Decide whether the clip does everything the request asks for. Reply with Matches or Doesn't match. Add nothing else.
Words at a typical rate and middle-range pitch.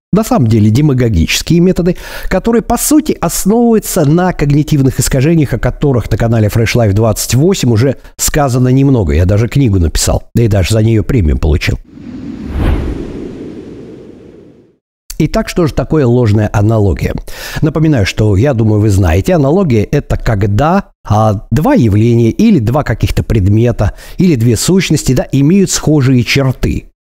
Doesn't match